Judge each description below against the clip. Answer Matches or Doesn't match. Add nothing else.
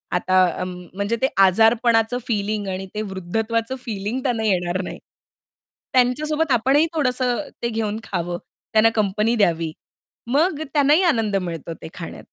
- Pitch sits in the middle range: Doesn't match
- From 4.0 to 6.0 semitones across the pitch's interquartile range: Matches